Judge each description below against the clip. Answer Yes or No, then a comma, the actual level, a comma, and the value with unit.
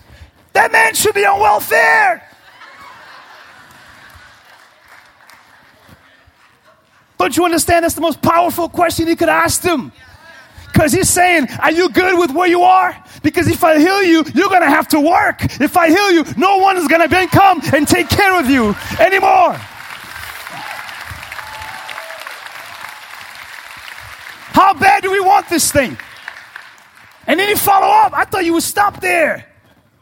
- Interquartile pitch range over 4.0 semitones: No, average, 2.8 semitones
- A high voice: Yes, very high, 350 Hz